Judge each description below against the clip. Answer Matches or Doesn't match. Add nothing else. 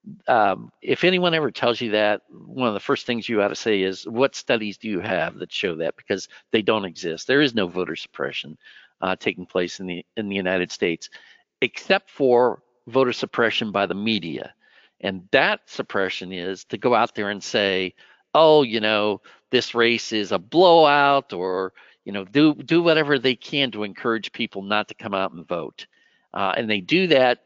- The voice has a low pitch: Matches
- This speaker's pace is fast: Doesn't match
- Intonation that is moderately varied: Doesn't match